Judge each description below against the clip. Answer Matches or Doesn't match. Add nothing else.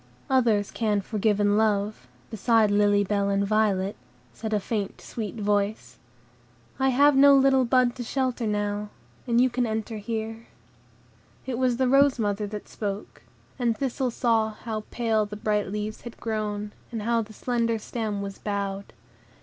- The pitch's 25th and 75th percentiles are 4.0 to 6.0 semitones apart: Doesn't match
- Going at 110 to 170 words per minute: Matches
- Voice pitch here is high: Matches